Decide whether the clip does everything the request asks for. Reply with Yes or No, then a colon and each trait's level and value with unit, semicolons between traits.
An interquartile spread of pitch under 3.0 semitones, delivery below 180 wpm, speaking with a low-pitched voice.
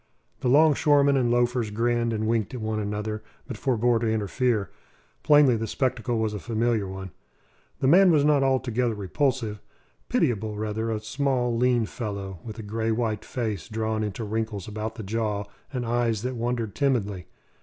Yes: narrow, 2.5 semitones; average, 165 wpm; low, 115 Hz